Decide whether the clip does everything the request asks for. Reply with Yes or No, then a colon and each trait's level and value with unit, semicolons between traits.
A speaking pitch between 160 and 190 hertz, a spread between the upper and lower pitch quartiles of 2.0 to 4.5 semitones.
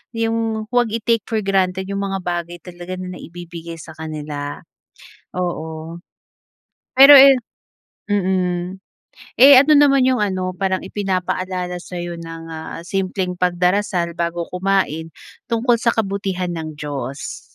Yes: medium, 185 Hz; average, 3.2 semitones